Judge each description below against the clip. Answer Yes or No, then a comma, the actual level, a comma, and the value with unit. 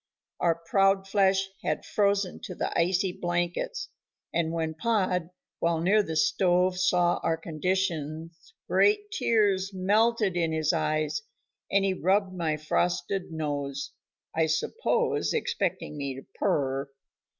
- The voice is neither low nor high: Yes, medium, 180 Hz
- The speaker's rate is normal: No, slow, 130 wpm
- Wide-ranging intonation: No, average, 3.4 semitones